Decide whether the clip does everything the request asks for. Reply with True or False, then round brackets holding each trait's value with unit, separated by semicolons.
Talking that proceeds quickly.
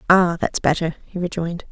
False (175 wpm)